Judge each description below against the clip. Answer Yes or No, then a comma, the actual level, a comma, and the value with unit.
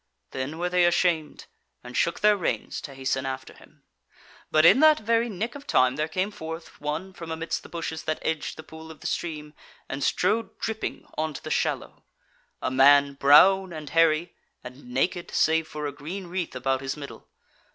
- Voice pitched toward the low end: No, medium, 160 Hz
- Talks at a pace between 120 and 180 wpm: No, average, 190 wpm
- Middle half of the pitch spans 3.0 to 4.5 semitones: Yes, average, 4.0 semitones